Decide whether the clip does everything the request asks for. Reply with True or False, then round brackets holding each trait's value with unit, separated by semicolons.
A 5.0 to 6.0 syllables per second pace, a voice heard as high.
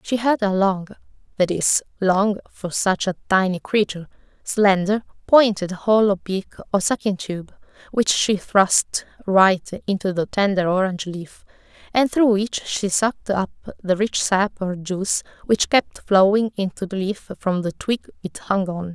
False (4.7 syllables/s; 195 Hz)